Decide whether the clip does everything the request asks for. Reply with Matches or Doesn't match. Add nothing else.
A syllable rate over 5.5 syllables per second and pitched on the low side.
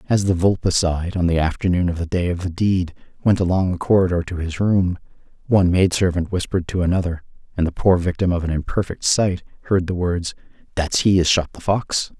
Matches